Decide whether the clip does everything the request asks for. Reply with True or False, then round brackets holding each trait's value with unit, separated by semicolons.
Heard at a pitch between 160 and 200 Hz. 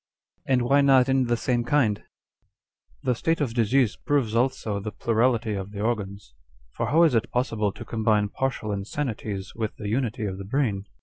False (115 Hz)